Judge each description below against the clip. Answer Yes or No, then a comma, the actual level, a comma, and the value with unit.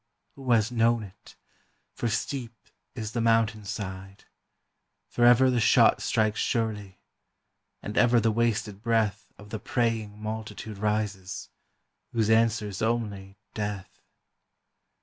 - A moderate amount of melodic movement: No, narrow, 2.0 semitones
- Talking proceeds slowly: Yes, slow, 120 wpm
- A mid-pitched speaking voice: No, low, 110 Hz